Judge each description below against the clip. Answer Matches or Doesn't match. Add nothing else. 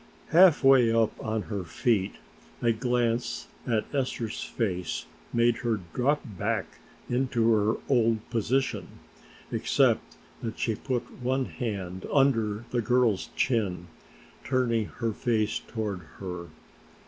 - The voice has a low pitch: Matches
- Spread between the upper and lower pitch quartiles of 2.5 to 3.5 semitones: Matches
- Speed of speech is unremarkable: Doesn't match